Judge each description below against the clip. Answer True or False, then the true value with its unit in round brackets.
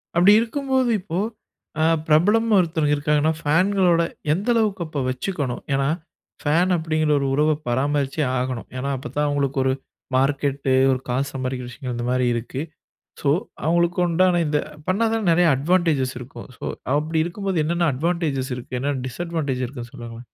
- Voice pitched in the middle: True (150 Hz)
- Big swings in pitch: False (4.7 semitones)